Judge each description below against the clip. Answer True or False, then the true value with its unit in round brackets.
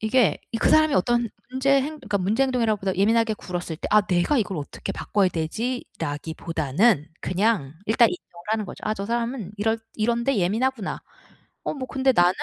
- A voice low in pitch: False (215 Hz)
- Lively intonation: False (5.0 semitones)